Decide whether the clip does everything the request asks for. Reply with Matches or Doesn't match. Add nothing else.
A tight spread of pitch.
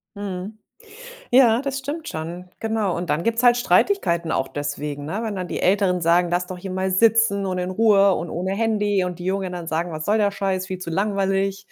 Doesn't match